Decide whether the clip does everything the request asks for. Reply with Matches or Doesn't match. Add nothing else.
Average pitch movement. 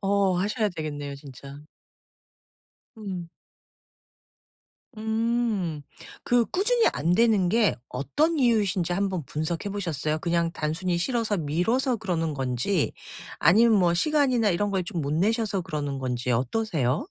Doesn't match